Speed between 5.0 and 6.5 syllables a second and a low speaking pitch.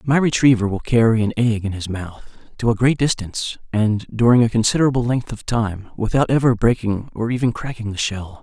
Yes: 5.5 syllables/s; low, 115 Hz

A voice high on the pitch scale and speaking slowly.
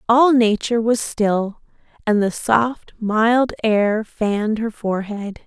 Yes: high, 220 Hz; slow, 130 wpm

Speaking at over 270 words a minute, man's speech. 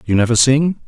No: fast, 205 wpm; male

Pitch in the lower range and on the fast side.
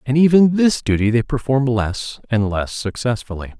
No: low, 125 Hz; average, 165 wpm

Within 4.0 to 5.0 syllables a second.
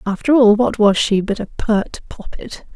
Yes: 4.6 syllables/s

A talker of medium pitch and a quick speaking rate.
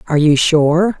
No: medium, 160 Hz; average, 180 wpm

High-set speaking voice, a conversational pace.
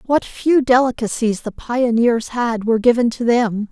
Yes: high, 235 Hz; average, 160 wpm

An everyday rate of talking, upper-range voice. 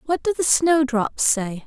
Yes: average, 180 wpm; very high, 275 Hz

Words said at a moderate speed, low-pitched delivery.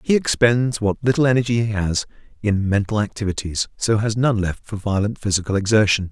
Yes: average, 175 wpm; low, 105 Hz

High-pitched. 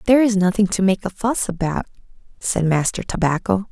Yes: high, 195 Hz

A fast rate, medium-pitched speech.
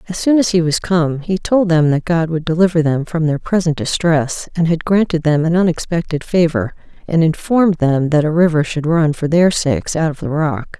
Yes: fast, 220 wpm; medium, 165 Hz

